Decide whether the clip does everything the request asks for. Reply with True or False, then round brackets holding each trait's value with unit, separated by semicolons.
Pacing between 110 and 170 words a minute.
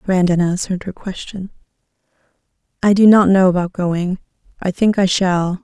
True (150 wpm)